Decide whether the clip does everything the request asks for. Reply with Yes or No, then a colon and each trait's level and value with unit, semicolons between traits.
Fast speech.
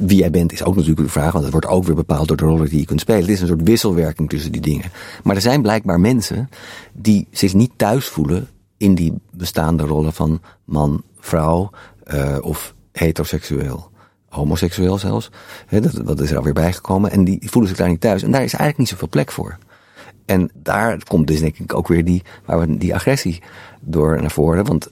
Yes: fast, 215 wpm